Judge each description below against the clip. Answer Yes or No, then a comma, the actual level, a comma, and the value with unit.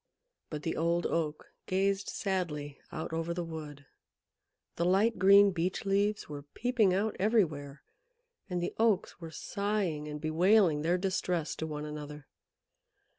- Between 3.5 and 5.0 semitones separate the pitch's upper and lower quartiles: Yes, average, 4.6 semitones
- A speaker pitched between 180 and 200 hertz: No, medium, 170 Hz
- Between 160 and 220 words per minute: No, average, 140 wpm